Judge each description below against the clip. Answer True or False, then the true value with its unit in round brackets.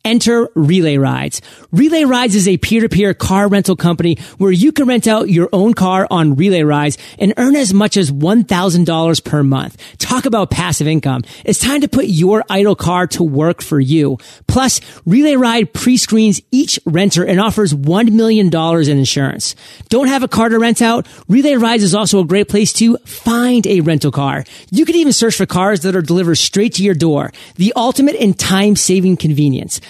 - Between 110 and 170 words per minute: False (190 wpm)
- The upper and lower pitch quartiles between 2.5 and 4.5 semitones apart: False (5.5 semitones)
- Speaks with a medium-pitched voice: False (195 Hz)